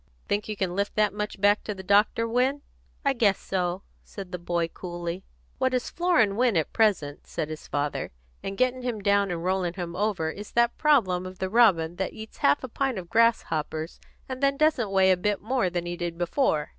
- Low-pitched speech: No, high, 200 Hz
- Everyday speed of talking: No, fast, 210 wpm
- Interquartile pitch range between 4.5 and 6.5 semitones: Yes, average, 4.8 semitones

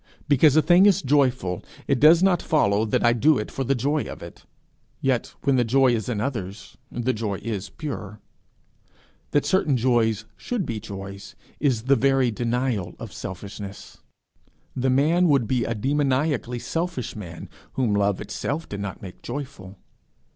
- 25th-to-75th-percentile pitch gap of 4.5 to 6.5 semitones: Yes, average, 5.1 semitones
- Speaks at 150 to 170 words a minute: Yes, average, 165 wpm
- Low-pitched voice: Yes, low, 125 Hz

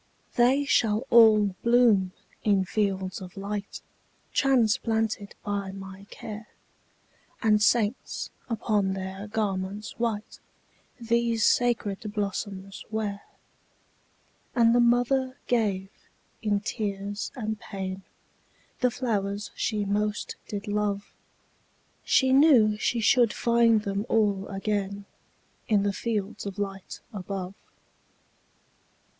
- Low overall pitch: No, high, 210 Hz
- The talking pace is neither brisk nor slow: No, slow, 105 wpm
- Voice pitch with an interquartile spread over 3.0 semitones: No, narrow, 2.5 semitones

